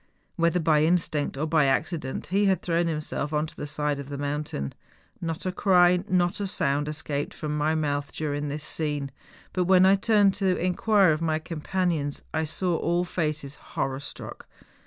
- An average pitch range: Yes, average, 3.5 semitones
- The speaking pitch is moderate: Yes, medium, 160 Hz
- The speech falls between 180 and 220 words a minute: Yes, average, 190 wpm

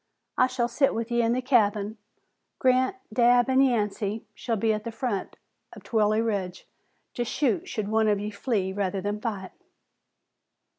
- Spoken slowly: No, average, 165 wpm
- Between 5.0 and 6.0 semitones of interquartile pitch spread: No, average, 2.9 semitones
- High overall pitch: Yes, high, 225 Hz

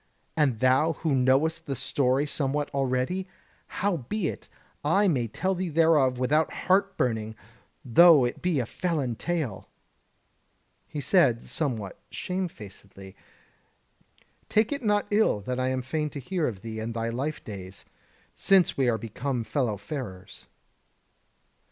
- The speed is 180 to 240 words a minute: No, average, 140 wpm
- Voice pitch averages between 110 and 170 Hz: Yes, low, 135 Hz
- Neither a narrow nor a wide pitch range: No, wide, 5.9 semitones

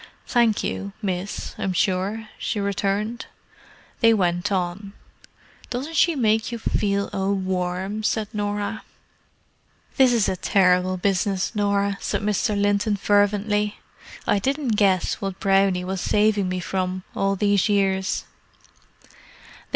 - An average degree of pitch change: No, narrow, 1.9 semitones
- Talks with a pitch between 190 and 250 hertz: Yes, high, 200 Hz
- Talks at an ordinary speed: No, slow, 125 wpm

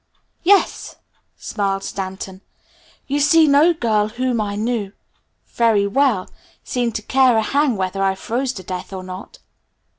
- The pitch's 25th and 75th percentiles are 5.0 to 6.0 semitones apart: Yes, average, 5.3 semitones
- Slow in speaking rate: No, average, 145 wpm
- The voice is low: No, high, 220 Hz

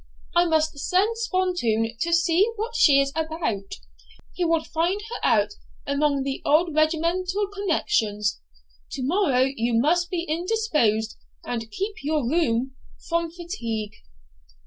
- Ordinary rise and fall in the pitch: No, wide, 6.2 semitones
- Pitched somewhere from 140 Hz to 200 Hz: No, very high, 320 Hz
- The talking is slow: Yes, slow, 130 wpm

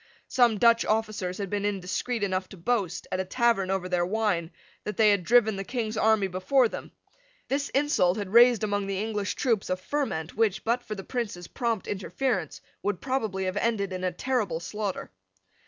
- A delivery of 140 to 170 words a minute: No, average, 190 wpm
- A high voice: Yes, high, 205 Hz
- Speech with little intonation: No, average, 3.8 semitones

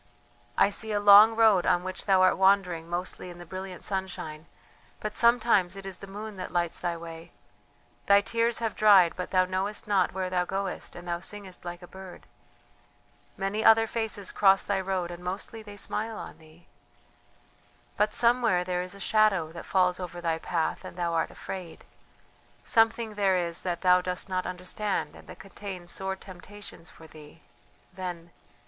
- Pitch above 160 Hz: Yes, high, 190 Hz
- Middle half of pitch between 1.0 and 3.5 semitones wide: Yes, average, 2.7 semitones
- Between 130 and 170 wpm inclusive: No, average, 180 wpm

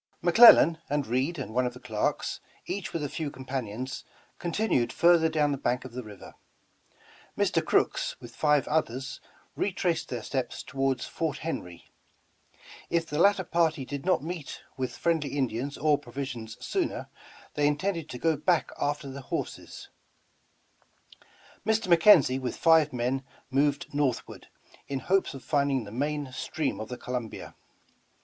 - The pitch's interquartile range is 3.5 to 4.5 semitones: Yes, average, 4.2 semitones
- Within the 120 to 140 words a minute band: No, average, 150 wpm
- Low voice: No, medium, 145 Hz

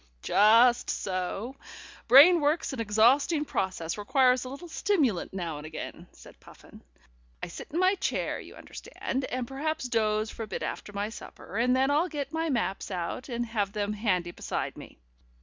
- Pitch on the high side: Yes, high, 240 Hz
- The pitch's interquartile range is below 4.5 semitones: No, average, 5.3 semitones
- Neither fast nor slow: Yes, average, 175 wpm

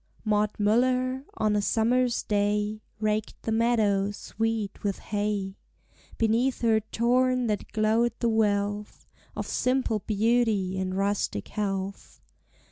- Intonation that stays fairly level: Yes, narrow, 2.3 semitones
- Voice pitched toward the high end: Yes, high, 215 Hz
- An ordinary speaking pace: No, slow, 120 wpm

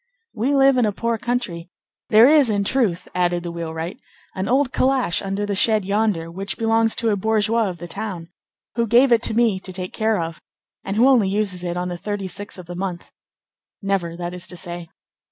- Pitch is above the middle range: Yes, high, 200 Hz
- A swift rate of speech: Yes, fast, 210 wpm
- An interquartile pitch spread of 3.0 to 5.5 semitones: Yes, average, 4.3 semitones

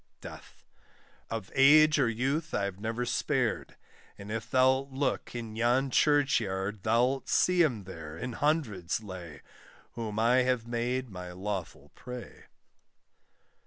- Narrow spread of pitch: No, average, 4.5 semitones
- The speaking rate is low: Yes, slow, 130 wpm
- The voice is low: Yes, low, 115 Hz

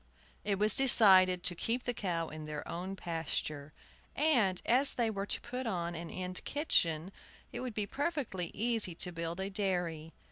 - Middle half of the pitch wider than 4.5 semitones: Yes, average, 5.2 semitones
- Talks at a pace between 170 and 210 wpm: Yes, average, 175 wpm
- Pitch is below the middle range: No, high, 190 Hz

